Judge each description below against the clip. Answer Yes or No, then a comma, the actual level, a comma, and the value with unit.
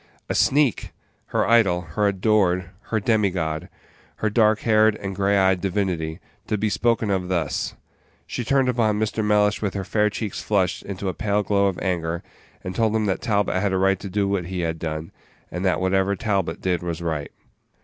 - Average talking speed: Yes, average, 190 wpm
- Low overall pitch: Yes, low, 100 Hz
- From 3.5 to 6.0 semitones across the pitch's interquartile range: No, average, 2.8 semitones